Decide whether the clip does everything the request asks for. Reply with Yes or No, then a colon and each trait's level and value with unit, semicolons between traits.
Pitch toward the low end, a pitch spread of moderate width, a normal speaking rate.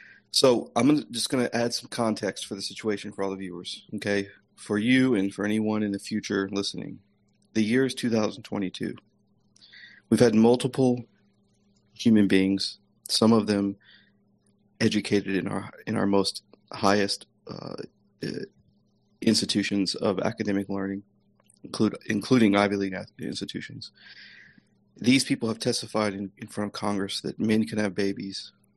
No: low, 105 Hz; narrow, 2.0 semitones; average, 145 wpm